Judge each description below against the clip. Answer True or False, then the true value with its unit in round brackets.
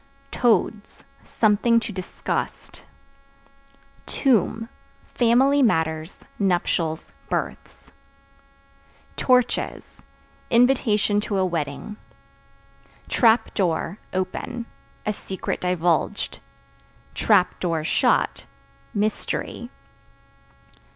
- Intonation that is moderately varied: True (4.6 semitones)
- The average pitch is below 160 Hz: False (210 Hz)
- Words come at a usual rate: False (65 wpm)